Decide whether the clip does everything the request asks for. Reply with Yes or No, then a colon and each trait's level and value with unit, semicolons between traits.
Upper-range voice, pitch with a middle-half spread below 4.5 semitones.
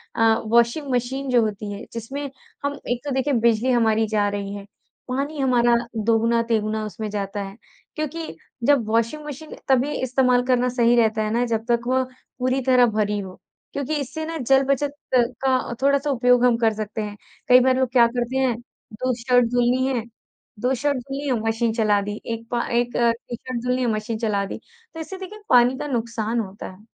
Yes: high, 240 Hz; average, 2.9 semitones